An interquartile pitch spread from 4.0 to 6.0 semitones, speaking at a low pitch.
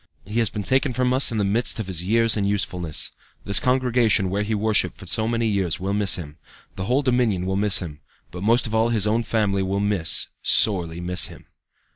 No: average, 3.3 semitones; low, 105 Hz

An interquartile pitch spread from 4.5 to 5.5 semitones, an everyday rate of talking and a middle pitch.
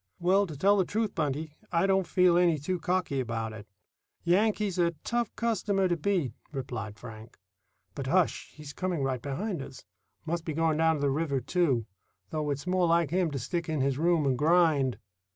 Yes: average, 4.8 semitones; average, 190 wpm; medium, 160 Hz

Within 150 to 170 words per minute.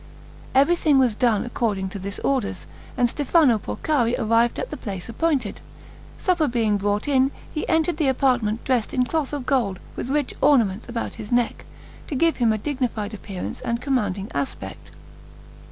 Yes: average, 165 wpm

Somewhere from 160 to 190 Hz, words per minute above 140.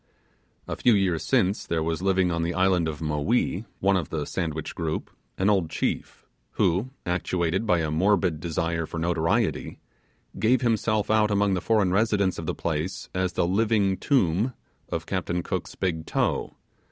No: very low, 90 Hz; average, 165 wpm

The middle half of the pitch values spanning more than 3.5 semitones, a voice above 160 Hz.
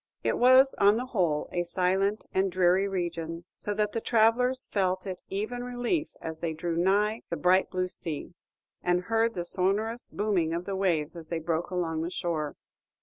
Yes: average, 3.9 semitones; medium, 185 Hz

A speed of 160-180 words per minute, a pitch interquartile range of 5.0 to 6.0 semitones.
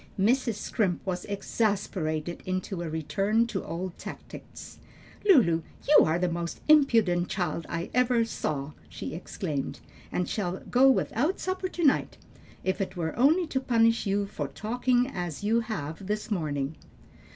No: average, 150 wpm; wide, 5.6 semitones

